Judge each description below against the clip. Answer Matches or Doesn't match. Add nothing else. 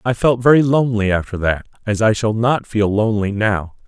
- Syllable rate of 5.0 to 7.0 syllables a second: Matches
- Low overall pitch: Matches